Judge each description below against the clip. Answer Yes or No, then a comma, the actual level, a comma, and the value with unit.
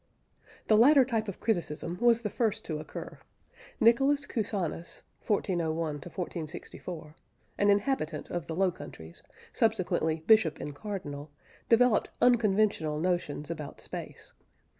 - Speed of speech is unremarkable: No, slow, 120 wpm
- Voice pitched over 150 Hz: Yes, medium, 185 Hz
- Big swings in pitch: Yes, wide, 5.9 semitones